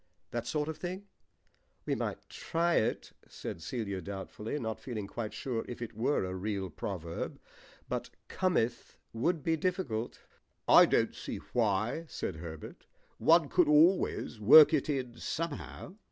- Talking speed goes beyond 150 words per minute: No, average, 145 wpm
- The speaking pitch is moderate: No, low, 120 Hz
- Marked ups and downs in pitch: Yes, wide, 7.2 semitones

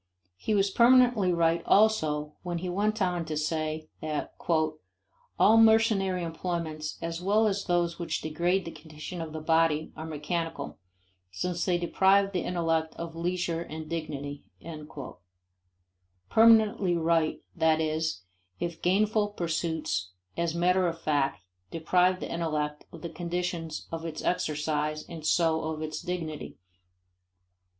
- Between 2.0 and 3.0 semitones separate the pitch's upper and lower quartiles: Yes, narrow, 2.5 semitones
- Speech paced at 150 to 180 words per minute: No, slow, 135 wpm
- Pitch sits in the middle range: Yes, medium, 165 Hz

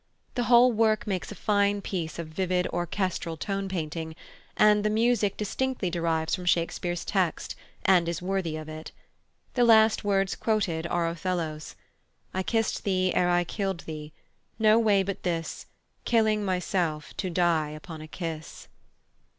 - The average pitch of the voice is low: No, medium, 185 Hz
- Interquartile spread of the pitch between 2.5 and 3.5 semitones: No, average, 3.9 semitones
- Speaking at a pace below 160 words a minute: Yes, average, 150 wpm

